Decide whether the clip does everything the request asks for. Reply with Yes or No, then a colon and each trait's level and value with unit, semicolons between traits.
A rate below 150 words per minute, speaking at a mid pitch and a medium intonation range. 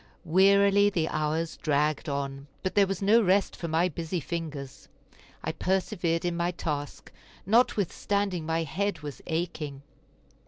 Yes: slow, 135 wpm; medium, 170 Hz; average, 4.1 semitones